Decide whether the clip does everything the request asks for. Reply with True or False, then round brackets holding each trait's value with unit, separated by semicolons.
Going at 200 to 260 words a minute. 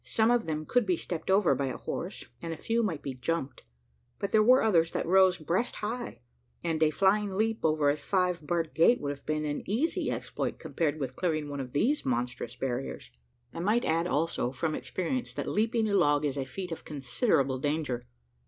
True (205 wpm)